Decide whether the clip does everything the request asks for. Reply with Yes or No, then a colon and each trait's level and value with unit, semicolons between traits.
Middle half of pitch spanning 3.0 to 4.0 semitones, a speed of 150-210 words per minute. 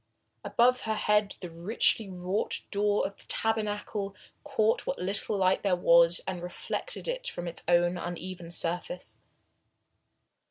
No: average, 3.3 semitones; slow, 135 wpm